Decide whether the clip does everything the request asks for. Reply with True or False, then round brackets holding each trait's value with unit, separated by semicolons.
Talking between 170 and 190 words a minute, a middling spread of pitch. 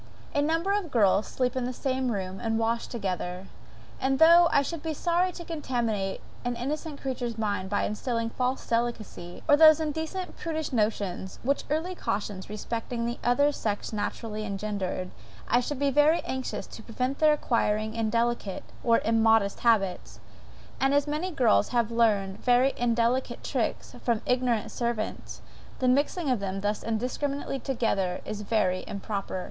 False (155 wpm; 4.8 semitones)